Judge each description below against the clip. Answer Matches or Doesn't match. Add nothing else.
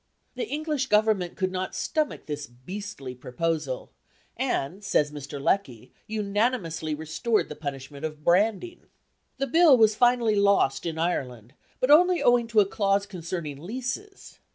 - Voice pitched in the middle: Doesn't match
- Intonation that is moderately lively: Doesn't match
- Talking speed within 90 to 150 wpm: Matches